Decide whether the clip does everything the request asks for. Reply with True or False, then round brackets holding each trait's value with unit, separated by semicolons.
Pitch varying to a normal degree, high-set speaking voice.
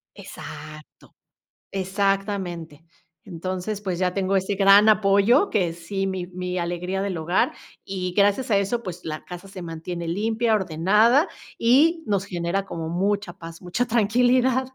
True (3.1 semitones; 195 Hz)